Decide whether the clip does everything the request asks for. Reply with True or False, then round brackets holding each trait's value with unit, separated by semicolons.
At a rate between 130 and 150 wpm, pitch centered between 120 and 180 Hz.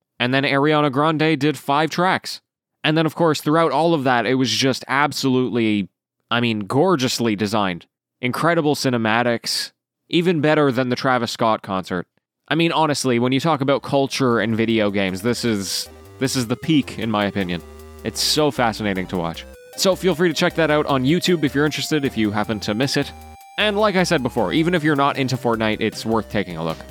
False (205 wpm; 130 Hz)